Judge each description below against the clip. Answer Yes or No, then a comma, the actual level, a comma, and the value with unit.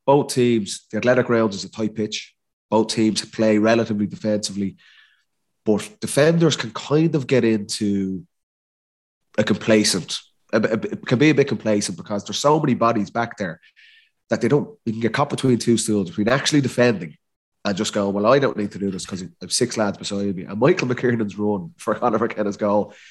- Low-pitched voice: Yes, low, 110 Hz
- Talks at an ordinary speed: Yes, average, 195 wpm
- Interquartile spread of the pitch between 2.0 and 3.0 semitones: No, average, 3.7 semitones